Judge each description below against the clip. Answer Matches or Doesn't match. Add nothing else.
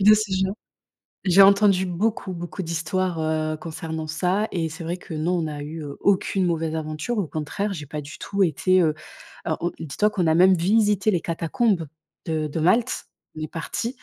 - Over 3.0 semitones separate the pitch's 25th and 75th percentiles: Matches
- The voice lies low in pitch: Doesn't match